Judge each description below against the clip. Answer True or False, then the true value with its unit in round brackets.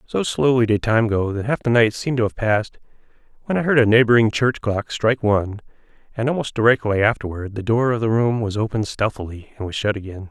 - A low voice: True (110 Hz)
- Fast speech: True (220 wpm)